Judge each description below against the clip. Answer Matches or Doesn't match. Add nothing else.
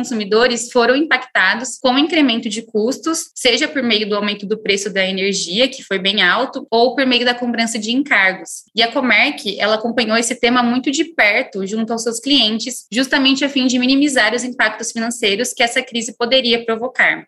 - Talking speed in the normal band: Doesn't match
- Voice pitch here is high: Matches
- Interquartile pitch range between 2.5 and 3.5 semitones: Matches